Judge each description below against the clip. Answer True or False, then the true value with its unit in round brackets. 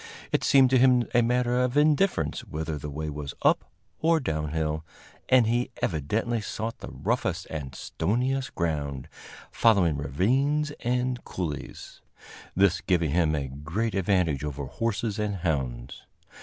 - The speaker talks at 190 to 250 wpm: False (140 wpm)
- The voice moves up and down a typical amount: False (8.4 semitones)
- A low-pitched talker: True (95 Hz)